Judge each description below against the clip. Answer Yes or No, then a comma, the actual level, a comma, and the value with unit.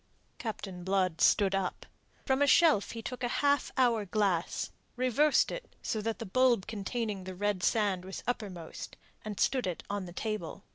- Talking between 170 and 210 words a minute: Yes, average, 175 wpm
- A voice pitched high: Yes, high, 210 Hz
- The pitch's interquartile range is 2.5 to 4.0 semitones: No, average, 4.6 semitones